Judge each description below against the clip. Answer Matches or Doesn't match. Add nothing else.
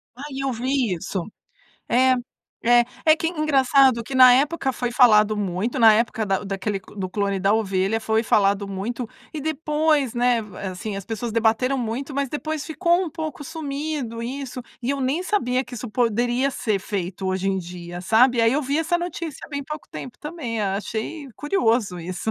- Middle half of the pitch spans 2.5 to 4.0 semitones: Doesn't match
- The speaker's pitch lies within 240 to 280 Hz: Matches